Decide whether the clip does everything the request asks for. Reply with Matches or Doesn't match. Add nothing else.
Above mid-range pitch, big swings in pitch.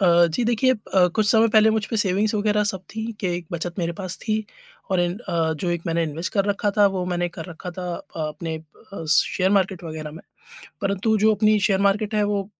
Doesn't match